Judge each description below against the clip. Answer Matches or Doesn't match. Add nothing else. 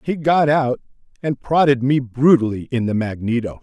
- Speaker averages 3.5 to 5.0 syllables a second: Matches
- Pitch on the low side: Matches